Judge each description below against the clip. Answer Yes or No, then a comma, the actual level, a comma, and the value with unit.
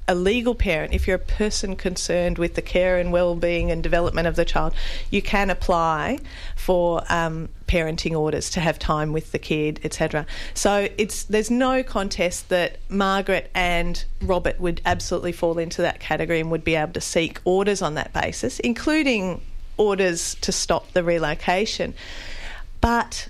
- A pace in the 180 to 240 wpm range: No, average, 165 wpm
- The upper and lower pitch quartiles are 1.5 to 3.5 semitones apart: Yes, average, 2.9 semitones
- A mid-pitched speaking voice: Yes, medium, 175 Hz